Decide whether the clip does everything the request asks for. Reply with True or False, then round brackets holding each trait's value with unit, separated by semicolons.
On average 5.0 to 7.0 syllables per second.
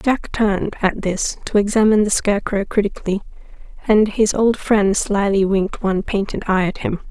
True (5.4 syllables/s)